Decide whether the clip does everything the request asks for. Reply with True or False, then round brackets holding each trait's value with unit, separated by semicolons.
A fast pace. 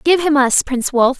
True (250 wpm)